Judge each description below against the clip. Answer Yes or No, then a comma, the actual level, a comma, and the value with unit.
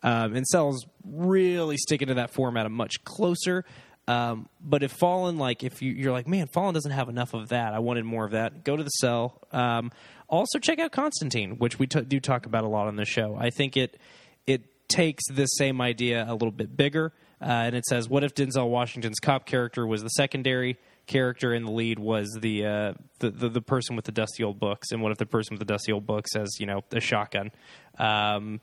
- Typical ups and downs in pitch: Yes, average, 3.9 semitones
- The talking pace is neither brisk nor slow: No, fast, 230 wpm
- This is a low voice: Yes, low, 120 Hz